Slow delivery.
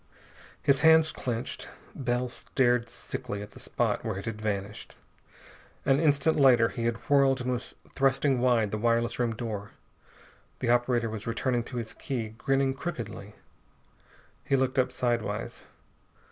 No: average, 145 wpm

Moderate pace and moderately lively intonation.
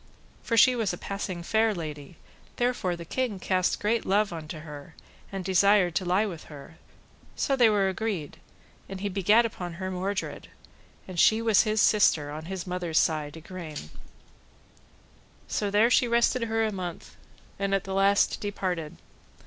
Yes: average, 165 wpm; average, 3.9 semitones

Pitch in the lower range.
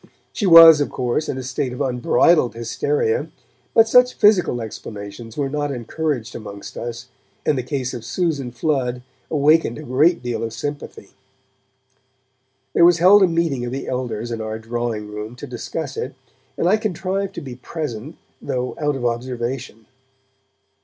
Yes: low, 130 Hz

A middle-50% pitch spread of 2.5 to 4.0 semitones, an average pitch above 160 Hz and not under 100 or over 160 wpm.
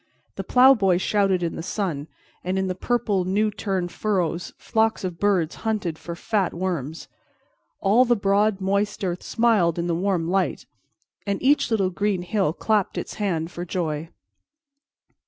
Yes: average, 3.2 semitones; high, 190 Hz; average, 155 wpm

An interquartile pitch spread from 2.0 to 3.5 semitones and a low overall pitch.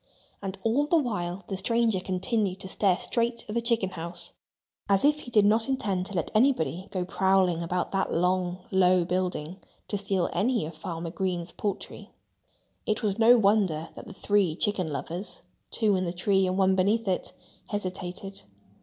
No: average, 3.0 semitones; high, 190 Hz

